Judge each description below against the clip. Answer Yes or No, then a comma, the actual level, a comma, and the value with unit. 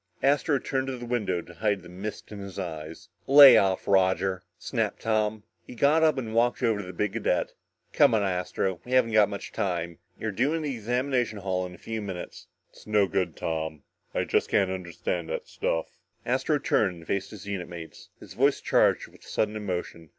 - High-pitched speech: No, low, 100 Hz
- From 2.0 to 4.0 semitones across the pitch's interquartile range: No, average, 4.7 semitones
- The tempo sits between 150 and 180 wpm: No, average, 200 wpm